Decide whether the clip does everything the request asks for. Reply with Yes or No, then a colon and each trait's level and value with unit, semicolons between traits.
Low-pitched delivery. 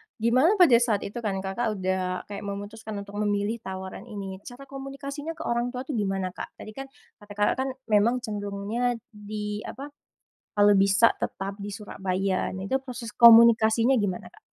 No: high, 210 Hz